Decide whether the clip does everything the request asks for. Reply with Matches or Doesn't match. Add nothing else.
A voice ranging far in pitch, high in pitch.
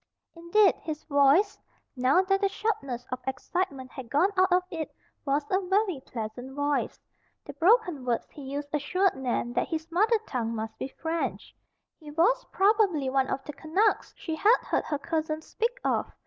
Matches